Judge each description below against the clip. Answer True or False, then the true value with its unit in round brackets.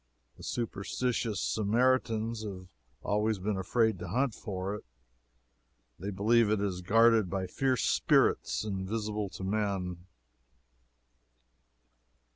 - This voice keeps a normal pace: False (105 wpm)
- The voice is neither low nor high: False (105 Hz)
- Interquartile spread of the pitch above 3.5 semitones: False (3.1 semitones)